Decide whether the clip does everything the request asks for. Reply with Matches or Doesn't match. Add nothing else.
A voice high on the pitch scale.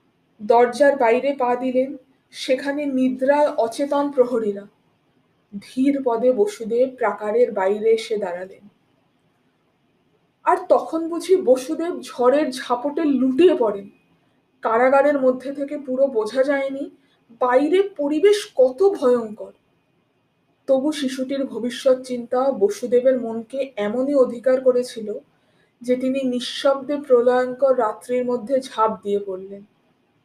Matches